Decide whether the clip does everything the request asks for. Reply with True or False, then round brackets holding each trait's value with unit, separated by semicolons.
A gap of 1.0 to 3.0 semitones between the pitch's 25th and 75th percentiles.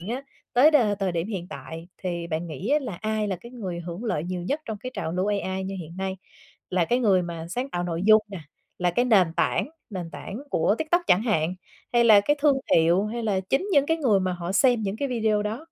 False (5.2 semitones)